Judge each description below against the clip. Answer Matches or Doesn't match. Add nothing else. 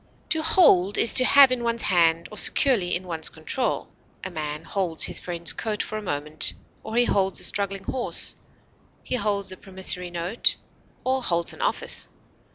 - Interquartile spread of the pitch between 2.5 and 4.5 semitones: Doesn't match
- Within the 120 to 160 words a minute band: Doesn't match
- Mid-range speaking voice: Doesn't match